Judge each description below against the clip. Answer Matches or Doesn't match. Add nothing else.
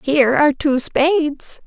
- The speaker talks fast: Doesn't match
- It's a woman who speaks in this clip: Matches